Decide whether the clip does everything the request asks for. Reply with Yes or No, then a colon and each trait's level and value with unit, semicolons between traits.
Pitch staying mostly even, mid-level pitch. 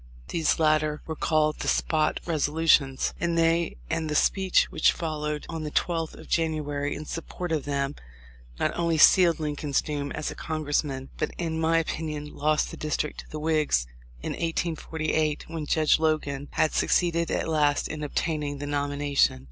Yes: narrow, 1.8 semitones; medium, 155 Hz